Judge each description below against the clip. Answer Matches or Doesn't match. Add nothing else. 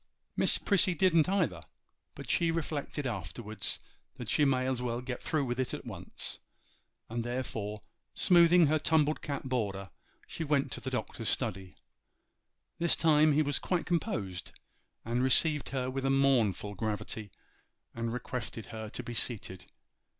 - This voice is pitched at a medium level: Doesn't match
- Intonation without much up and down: Doesn't match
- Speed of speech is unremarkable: Matches